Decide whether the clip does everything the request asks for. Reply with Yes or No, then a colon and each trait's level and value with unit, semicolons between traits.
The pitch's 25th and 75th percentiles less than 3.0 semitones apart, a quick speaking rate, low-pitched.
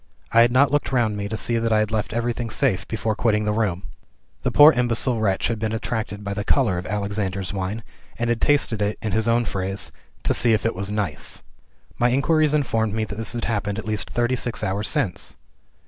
Yes: narrow, 2.6 semitones; fast, 225 wpm; low, 110 Hz